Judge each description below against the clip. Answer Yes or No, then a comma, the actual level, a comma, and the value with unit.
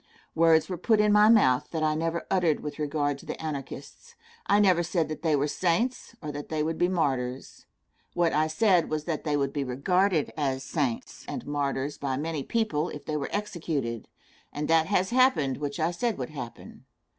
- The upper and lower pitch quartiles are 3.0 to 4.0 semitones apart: Yes, average, 3.7 semitones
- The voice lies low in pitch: No, medium, 155 Hz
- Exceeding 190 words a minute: Yes, average, 200 wpm